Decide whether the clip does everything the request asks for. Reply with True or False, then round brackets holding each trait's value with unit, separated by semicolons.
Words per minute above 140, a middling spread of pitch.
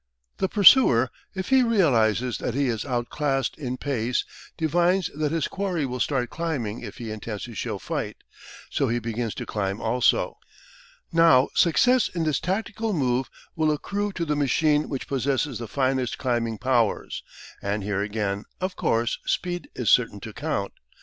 False (165 wpm; 6.2 semitones)